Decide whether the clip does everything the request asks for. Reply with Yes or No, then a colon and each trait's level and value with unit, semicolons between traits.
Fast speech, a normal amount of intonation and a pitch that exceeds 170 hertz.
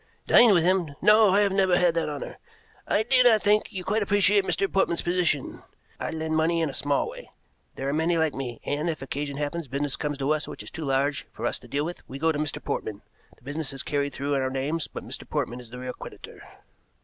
No: fast, 245 wpm; average, 4.7 semitones; medium, 160 Hz